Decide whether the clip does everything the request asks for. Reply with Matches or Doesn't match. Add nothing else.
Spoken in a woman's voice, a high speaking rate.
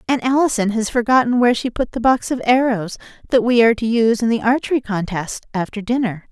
Matches